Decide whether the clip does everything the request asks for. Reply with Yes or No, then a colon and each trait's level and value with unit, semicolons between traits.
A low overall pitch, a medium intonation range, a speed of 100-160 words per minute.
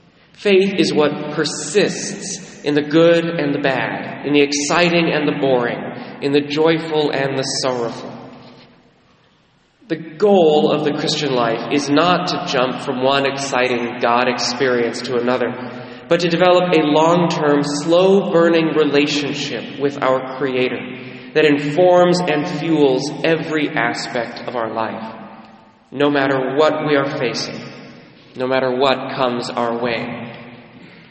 No: medium, 145 Hz; average, 3.7 semitones; average, 140 wpm